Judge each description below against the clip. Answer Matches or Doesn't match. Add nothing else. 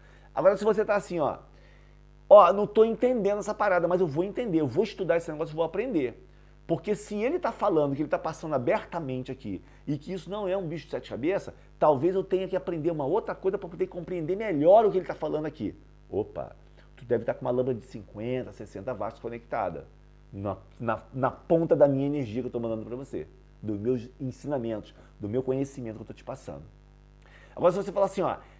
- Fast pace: Matches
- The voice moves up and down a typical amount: Doesn't match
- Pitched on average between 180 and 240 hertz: Doesn't match